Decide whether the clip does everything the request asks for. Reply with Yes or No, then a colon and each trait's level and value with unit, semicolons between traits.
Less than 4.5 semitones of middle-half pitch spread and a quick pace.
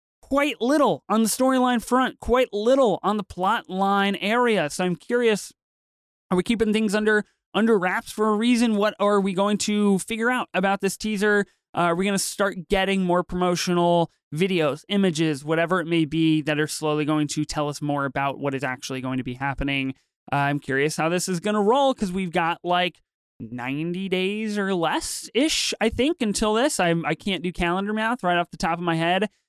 No: average, 4.9 semitones; fast, 210 wpm